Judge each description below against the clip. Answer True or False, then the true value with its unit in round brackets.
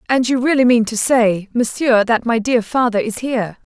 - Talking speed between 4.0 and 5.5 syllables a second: True (5.0 syllables/s)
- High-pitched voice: True (235 Hz)